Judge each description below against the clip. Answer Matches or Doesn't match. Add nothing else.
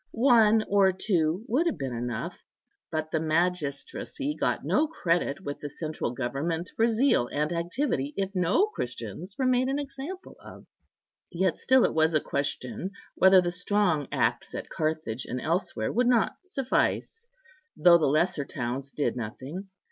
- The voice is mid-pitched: Matches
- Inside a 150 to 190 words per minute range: Matches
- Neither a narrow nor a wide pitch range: Doesn't match